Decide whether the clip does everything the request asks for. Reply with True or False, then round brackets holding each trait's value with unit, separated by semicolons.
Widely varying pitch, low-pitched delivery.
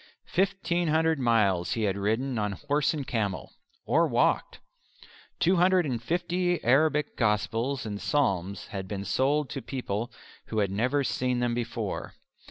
True (6.3 semitones; 125 Hz)